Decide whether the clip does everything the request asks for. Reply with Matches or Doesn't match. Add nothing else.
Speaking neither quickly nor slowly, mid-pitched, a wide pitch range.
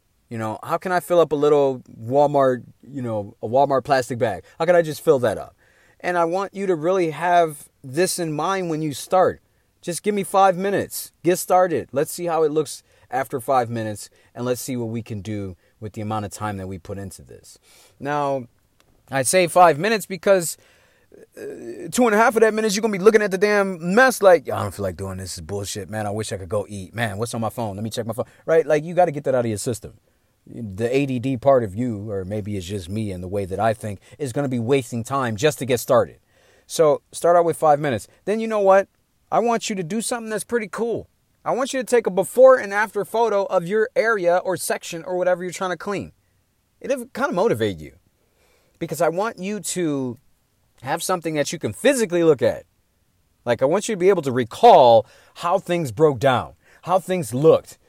Doesn't match